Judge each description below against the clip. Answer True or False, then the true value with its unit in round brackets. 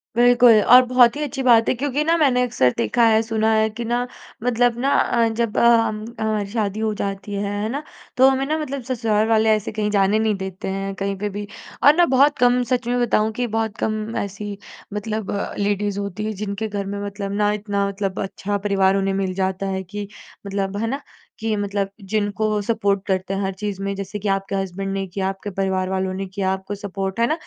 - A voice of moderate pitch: False (210 Hz)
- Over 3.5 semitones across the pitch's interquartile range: False (2.8 semitones)